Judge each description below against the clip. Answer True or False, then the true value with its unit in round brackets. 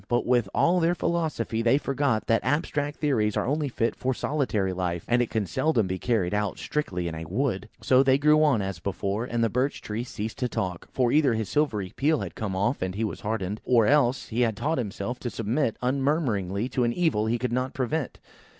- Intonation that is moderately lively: True (5.0 semitones)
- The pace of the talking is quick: True (220 wpm)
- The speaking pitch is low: True (120 Hz)